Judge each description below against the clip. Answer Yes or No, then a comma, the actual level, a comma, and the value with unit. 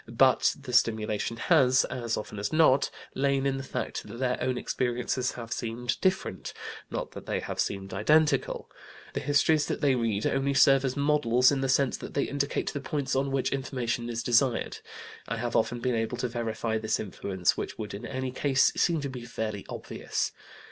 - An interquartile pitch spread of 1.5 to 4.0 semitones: Yes, average, 3.0 semitones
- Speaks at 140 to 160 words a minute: No, average, 190 wpm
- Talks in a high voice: No, low, 125 Hz